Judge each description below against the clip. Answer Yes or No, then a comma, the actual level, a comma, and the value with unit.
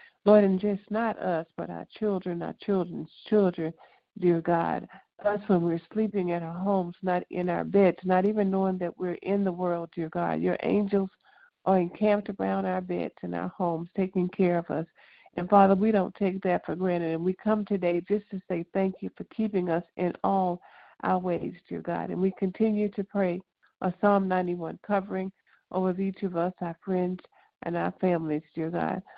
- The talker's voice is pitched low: No, medium, 185 Hz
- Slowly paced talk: No, average, 195 wpm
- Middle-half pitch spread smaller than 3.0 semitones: Yes, narrow, 2.5 semitones